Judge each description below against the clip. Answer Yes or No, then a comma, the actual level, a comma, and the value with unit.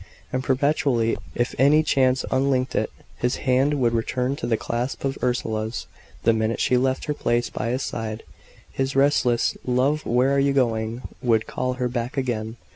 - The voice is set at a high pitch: No, low, 125 Hz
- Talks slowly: No, average, 175 wpm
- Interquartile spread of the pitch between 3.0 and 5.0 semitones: No, narrow, 2.4 semitones